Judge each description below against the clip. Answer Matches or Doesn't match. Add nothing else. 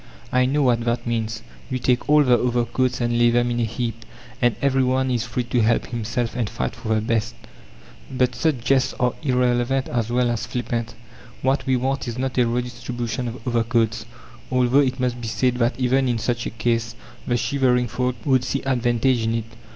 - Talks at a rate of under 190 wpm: Doesn't match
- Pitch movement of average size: Doesn't match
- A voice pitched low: Matches